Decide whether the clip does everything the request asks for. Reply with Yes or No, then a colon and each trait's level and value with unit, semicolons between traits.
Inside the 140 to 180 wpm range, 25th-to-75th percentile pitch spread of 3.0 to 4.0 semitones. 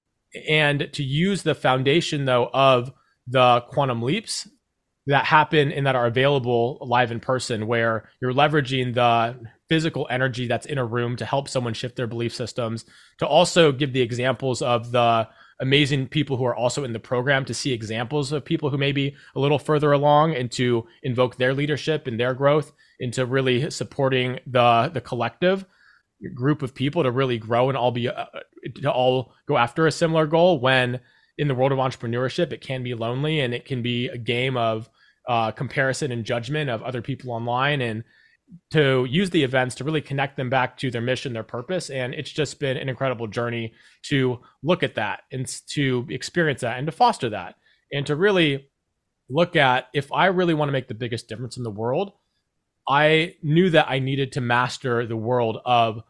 No: average, 195 wpm; average, 3.3 semitones